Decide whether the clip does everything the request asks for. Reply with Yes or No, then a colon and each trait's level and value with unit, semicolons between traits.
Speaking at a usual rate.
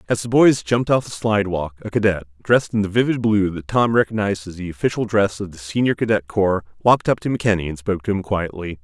No: fast, 240 wpm